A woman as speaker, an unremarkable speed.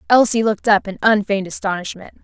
Yes: female; average, 160 wpm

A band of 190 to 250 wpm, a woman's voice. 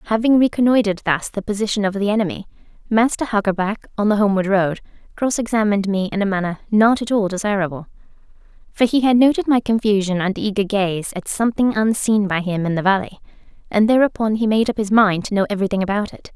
Yes: average, 195 wpm; female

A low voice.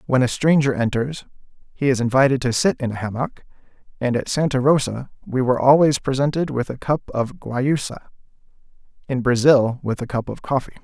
Yes: low, 130 Hz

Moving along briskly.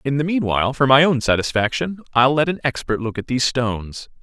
Yes: fast, 215 wpm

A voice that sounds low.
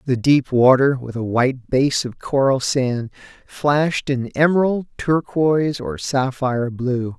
Yes: low, 130 Hz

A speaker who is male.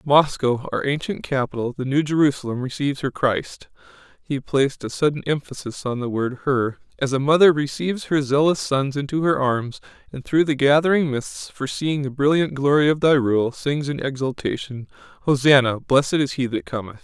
Yes: male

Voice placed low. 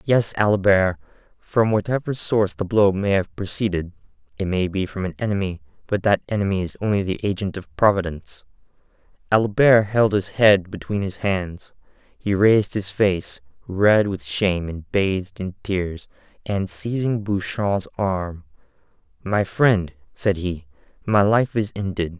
Yes: very low, 95 Hz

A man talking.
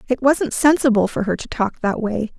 No: female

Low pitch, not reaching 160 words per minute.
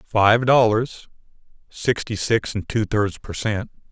Yes: low, 110 Hz; average, 140 wpm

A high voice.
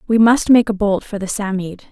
Yes: high, 210 Hz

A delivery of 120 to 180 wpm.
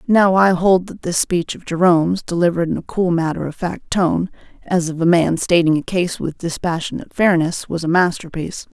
No: average, 200 wpm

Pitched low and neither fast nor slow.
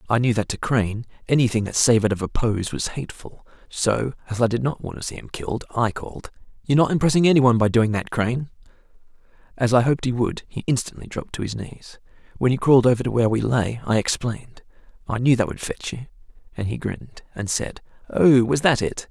No: low, 120 Hz; fast, 220 wpm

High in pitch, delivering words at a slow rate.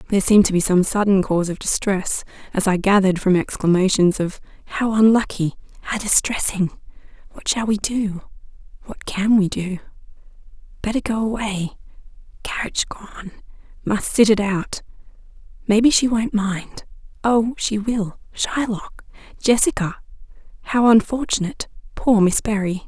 Yes: high, 205 Hz; slow, 100 wpm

